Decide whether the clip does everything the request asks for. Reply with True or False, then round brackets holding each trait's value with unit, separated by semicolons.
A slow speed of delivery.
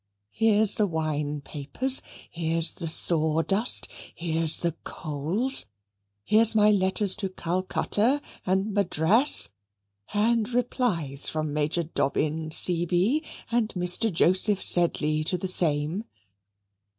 True (105 wpm)